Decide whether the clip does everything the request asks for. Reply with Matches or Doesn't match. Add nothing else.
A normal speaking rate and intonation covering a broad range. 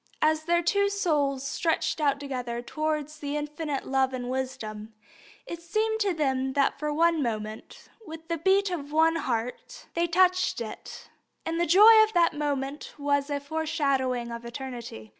Doesn't match